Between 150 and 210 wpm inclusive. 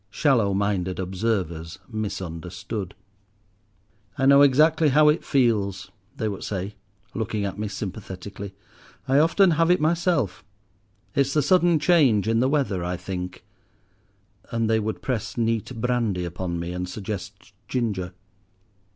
No: slow, 135 wpm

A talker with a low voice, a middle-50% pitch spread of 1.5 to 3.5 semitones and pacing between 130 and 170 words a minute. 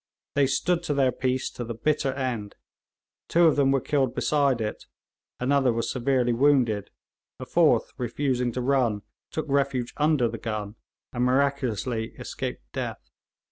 Yes: low, 130 Hz; average, 3.0 semitones; average, 150 wpm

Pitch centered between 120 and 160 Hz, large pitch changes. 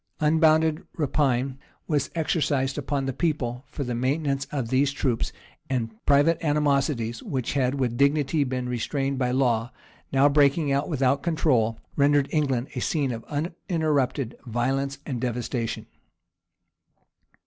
No: low, 135 Hz; average, 2.9 semitones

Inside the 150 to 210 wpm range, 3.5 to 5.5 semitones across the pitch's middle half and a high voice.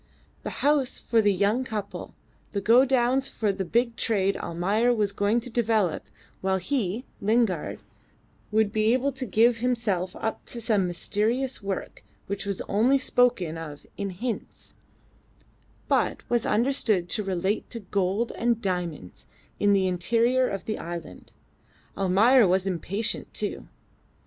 No: average, 140 wpm; average, 4.0 semitones; high, 215 Hz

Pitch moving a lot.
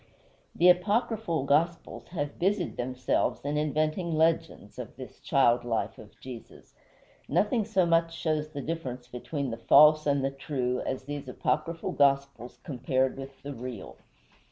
No: average, 4.2 semitones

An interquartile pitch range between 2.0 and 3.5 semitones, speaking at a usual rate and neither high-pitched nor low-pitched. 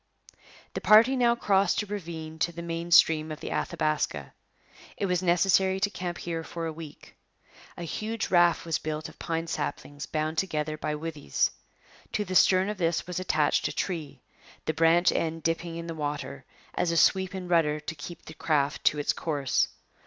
Yes: average, 2.9 semitones; average, 185 wpm; medium, 165 Hz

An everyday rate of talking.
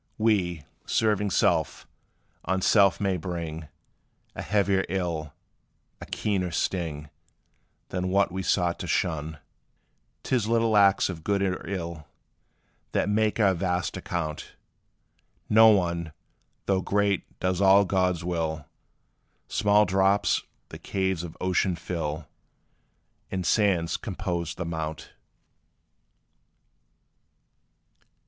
No: slow, 110 wpm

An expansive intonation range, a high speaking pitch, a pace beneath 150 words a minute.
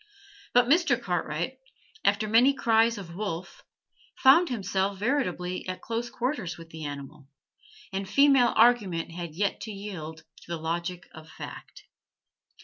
Yes: wide, 5.9 semitones; high, 195 Hz; slow, 135 wpm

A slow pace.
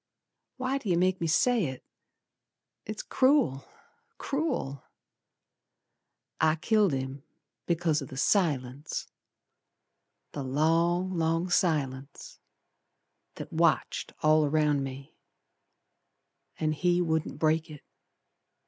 Yes: slow, 100 wpm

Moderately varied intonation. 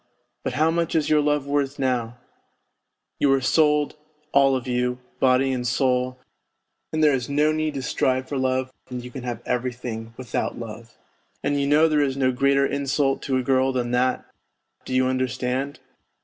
No: narrow, 2.2 semitones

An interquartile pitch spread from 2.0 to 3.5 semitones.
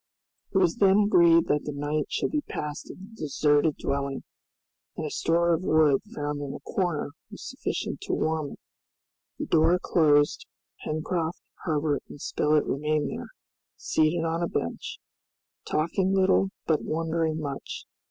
Yes: average, 2.7 semitones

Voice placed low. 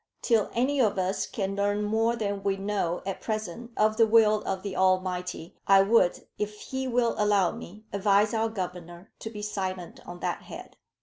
No: high, 205 Hz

